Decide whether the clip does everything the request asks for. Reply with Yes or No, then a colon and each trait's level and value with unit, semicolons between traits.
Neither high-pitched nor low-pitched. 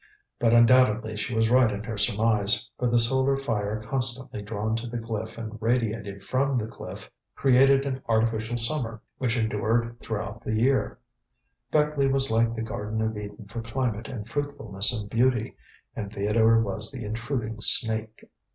No: low, 115 Hz